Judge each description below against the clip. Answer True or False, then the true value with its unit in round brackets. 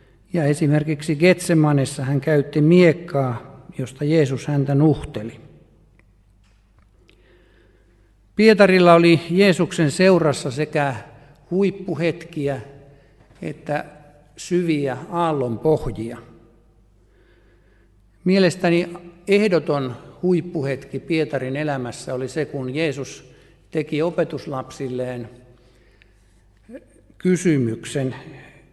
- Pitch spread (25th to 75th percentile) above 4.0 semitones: True (5.2 semitones)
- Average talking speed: False (65 wpm)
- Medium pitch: True (145 Hz)